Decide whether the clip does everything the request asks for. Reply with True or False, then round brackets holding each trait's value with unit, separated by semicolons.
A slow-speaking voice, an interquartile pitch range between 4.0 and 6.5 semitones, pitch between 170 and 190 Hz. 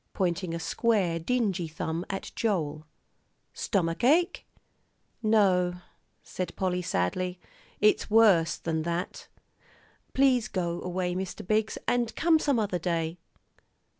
True (115 wpm; 4.4 semitones; 185 Hz)